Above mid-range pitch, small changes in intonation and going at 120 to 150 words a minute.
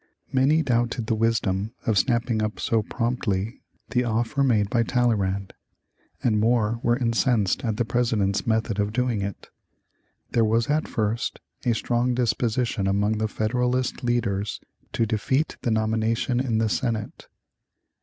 No: low, 115 Hz; narrow, 2.3 semitones; average, 145 wpm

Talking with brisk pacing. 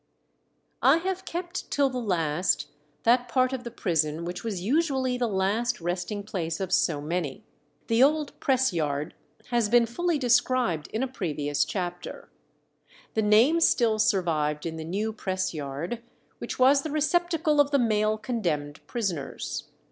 No: average, 155 wpm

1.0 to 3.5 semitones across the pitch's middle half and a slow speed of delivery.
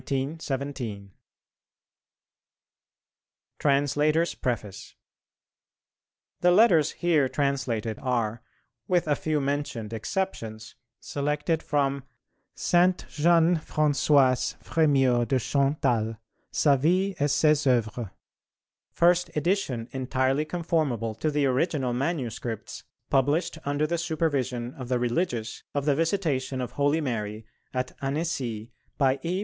No: average, 4.1 semitones; slow, 105 wpm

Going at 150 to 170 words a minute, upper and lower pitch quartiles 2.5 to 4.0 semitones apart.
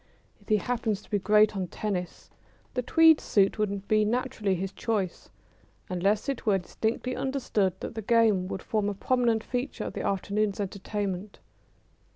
Yes: average, 165 wpm; average, 2.8 semitones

